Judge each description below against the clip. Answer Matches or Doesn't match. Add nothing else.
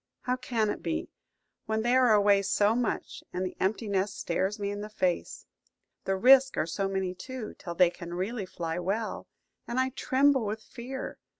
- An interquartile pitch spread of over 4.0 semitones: Matches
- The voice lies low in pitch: Doesn't match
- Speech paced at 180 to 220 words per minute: Matches